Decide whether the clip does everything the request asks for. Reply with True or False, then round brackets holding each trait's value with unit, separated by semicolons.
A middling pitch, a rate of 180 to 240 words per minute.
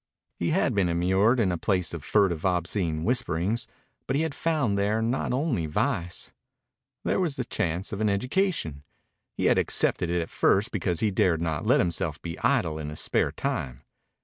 False (95 Hz; 185 wpm)